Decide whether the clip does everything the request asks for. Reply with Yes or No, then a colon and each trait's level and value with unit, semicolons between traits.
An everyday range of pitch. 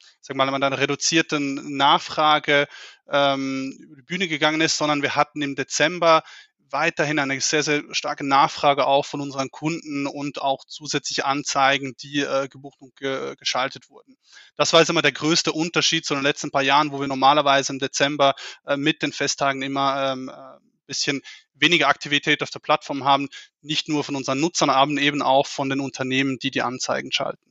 No: narrow, 1.7 semitones